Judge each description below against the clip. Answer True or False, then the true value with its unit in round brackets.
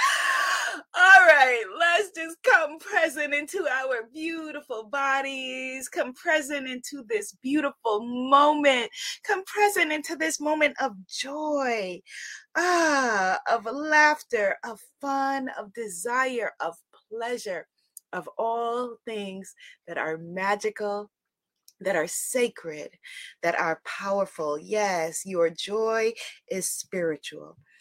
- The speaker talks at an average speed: False (105 wpm)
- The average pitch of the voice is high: True (260 Hz)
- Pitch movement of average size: False (6.4 semitones)